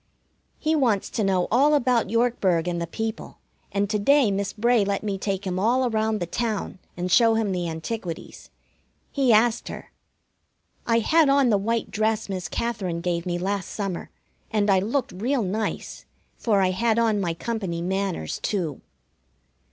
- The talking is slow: No, average, 170 wpm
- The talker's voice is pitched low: No, high, 205 Hz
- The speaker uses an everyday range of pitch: Yes, average, 3.9 semitones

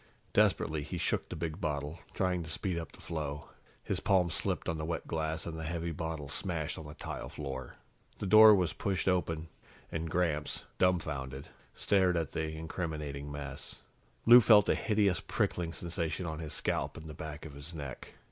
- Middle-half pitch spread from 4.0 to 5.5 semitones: No, average, 2.7 semitones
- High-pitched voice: No, very low, 80 Hz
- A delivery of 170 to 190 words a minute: Yes, average, 185 wpm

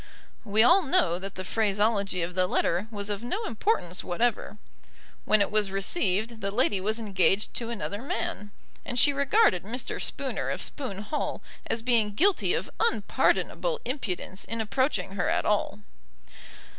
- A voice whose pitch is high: Yes, high, 210 Hz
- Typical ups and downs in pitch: Yes, average, 3.7 semitones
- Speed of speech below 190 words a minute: Yes, average, 155 wpm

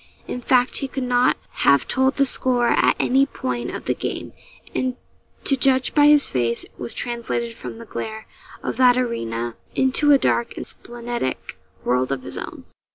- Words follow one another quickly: No, average, 175 wpm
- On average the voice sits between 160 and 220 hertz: No, high, 245 Hz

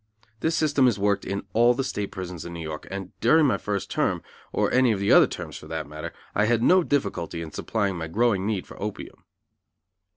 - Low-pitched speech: Yes, low, 100 Hz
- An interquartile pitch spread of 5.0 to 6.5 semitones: Yes, average, 5.3 semitones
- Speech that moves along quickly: Yes, fast, 220 wpm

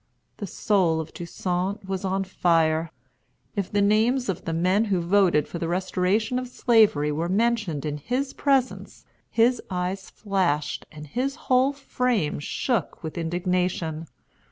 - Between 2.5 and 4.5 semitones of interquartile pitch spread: No, average, 5.3 semitones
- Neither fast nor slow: Yes, average, 145 wpm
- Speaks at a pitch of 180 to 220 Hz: Yes, high, 190 Hz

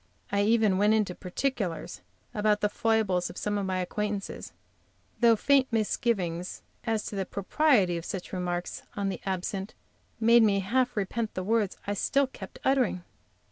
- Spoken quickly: No, average, 160 wpm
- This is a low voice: No, high, 205 Hz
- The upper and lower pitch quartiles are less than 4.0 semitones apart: Yes, average, 3.4 semitones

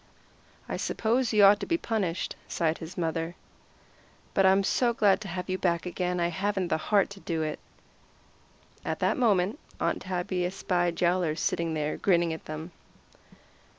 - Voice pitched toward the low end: No, medium, 180 Hz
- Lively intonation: No, average, 2.8 semitones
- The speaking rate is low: No, average, 165 wpm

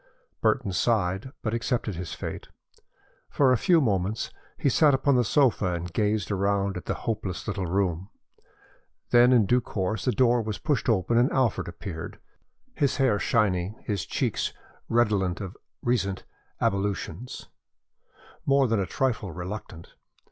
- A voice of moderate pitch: No, low, 105 Hz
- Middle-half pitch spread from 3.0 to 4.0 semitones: No, average, 4.4 semitones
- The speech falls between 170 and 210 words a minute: No, average, 145 wpm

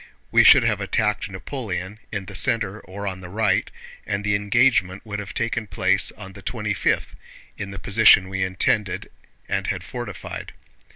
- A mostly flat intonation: Yes, narrow, 2.0 semitones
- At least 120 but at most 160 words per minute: No, average, 170 wpm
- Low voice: Yes, low, 100 Hz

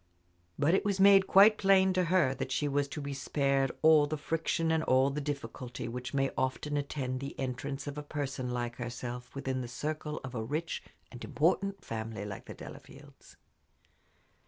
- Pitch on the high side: No, medium, 140 Hz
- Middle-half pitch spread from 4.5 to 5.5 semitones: No, average, 3.6 semitones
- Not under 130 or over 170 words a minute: No, average, 180 wpm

